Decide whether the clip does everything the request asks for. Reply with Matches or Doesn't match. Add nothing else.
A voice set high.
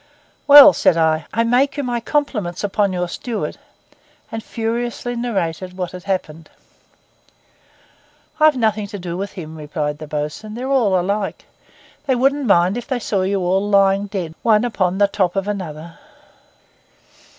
Matches